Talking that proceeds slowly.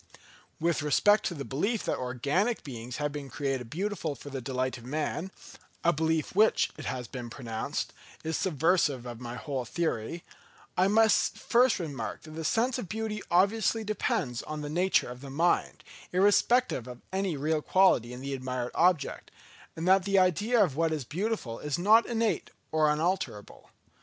No: average, 165 wpm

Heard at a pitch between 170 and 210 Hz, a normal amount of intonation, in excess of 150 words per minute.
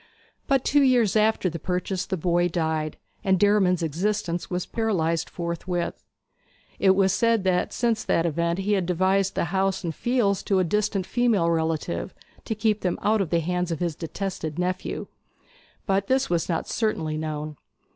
Yes: medium, 185 Hz; average, 3.5 semitones; average, 170 wpm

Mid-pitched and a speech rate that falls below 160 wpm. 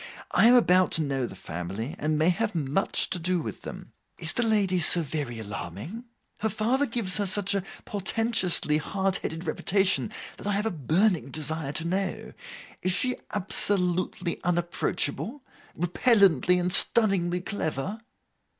Yes: medium, 180 Hz; average, 150 wpm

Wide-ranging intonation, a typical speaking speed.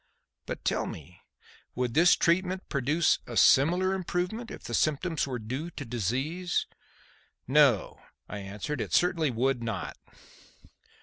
No: wide, 6.6 semitones; slow, 130 wpm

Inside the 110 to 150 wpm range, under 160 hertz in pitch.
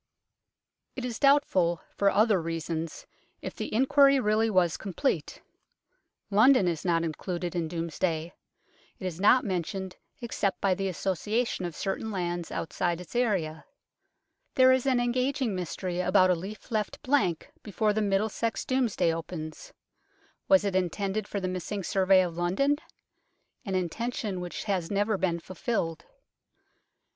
No: average, 140 wpm; high, 195 Hz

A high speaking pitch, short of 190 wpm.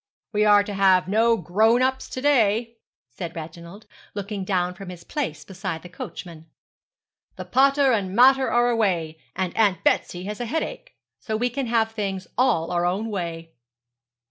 Yes: high, 205 Hz; average, 170 wpm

